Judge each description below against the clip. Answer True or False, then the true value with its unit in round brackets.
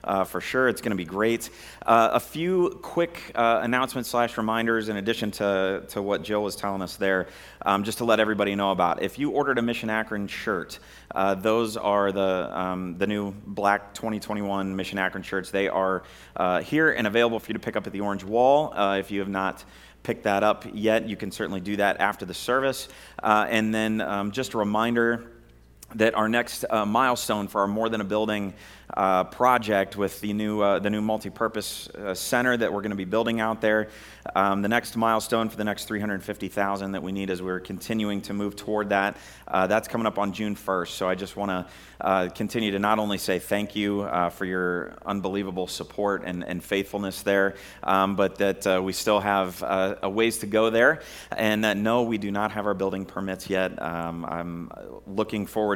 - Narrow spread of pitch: True (2.3 semitones)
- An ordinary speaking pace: False (210 wpm)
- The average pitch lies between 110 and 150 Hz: False (100 Hz)